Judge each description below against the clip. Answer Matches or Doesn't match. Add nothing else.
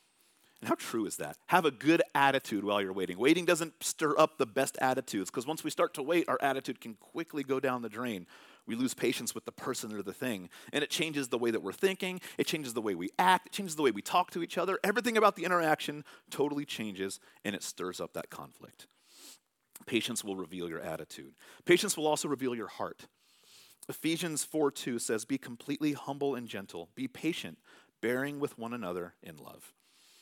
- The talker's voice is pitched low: Doesn't match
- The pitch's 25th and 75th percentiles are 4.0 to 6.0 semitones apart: Matches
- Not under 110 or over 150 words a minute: Doesn't match